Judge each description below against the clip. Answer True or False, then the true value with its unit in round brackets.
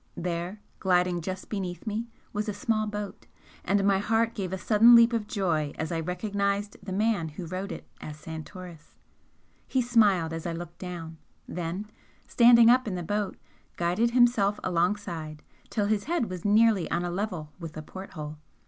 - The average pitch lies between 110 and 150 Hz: False (190 Hz)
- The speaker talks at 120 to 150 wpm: False (175 wpm)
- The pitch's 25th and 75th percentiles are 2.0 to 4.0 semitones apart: True (3.7 semitones)